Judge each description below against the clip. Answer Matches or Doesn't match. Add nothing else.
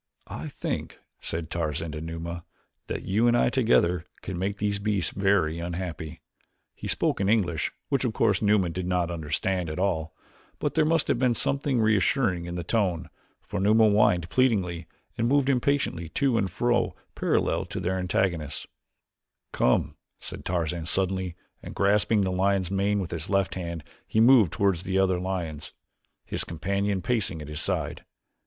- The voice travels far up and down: Doesn't match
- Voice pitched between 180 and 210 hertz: Doesn't match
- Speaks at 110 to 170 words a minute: Matches